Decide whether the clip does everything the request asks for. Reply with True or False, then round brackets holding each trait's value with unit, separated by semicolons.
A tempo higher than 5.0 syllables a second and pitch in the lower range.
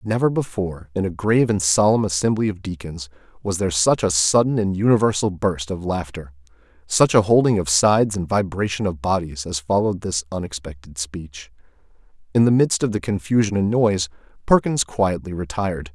True (5.5 syllables/s; 95 Hz)